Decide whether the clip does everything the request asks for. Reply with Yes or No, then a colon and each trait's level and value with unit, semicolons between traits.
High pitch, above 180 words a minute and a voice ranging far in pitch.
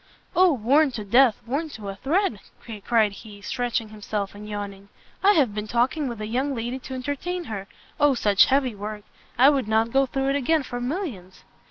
No: high, 240 Hz; average, 195 wpm; average, 4.7 semitones